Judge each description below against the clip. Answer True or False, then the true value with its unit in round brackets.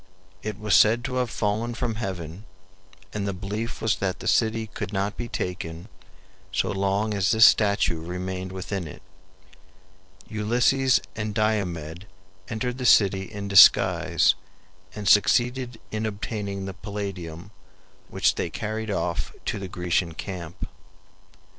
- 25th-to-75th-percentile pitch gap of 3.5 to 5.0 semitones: False (3.0 semitones)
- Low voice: True (100 Hz)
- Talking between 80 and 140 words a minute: True (135 wpm)